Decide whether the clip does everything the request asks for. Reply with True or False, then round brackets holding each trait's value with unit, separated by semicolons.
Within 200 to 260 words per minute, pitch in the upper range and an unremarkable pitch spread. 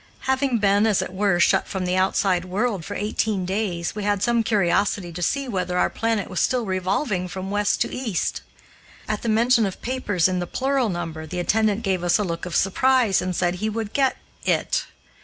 True (205 wpm; 200 Hz; 3.6 semitones)